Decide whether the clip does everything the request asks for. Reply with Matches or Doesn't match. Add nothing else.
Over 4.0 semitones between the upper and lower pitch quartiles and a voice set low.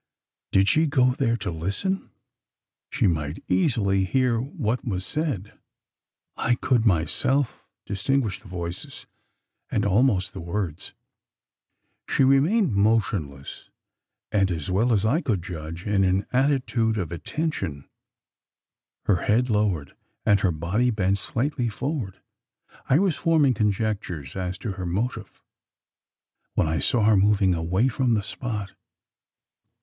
Matches